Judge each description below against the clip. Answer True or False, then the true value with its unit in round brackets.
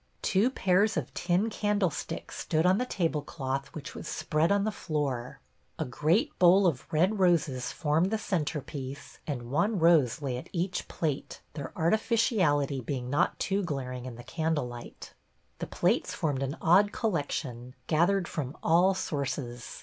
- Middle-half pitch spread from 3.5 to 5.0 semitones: False (5.6 semitones)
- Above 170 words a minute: False (155 wpm)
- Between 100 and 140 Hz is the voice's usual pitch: False (155 Hz)